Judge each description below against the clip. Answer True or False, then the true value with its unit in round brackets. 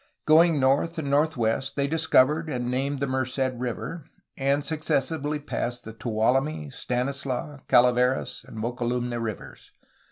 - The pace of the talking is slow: True (125 wpm)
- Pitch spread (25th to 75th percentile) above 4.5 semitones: False (3.3 semitones)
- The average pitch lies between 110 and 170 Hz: True (135 Hz)